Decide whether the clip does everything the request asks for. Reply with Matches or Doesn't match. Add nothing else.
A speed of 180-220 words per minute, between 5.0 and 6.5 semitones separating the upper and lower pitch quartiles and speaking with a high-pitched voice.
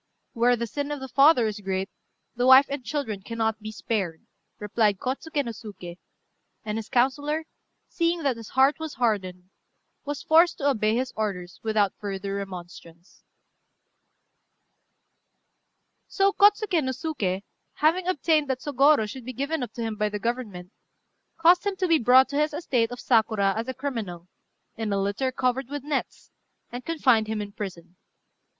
Doesn't match